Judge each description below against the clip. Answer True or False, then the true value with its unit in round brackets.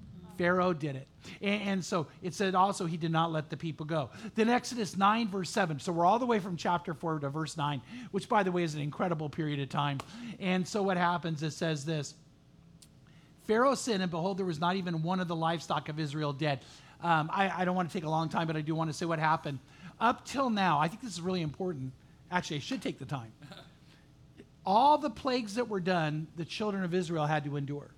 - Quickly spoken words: True (235 wpm)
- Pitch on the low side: False (170 Hz)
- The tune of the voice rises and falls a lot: False (3.8 semitones)